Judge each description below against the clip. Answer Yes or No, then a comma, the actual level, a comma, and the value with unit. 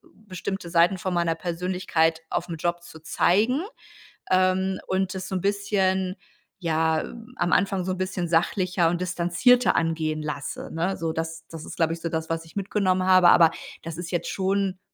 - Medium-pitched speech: Yes, medium, 175 Hz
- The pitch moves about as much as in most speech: No, narrow, 2.3 semitones